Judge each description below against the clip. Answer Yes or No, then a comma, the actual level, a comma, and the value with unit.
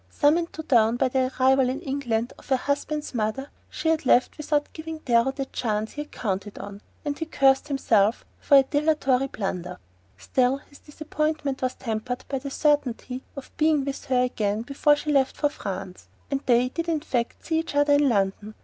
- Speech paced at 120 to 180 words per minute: No, average, 190 wpm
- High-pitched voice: Yes, very high, 270 Hz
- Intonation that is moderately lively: Yes, average, 3.8 semitones